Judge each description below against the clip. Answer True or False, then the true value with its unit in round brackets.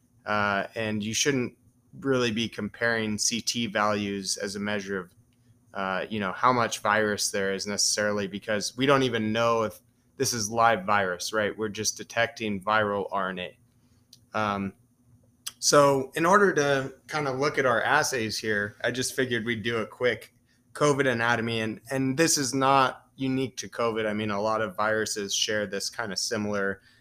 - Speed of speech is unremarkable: True (175 wpm)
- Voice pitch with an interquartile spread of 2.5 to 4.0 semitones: True (2.8 semitones)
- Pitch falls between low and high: False (115 Hz)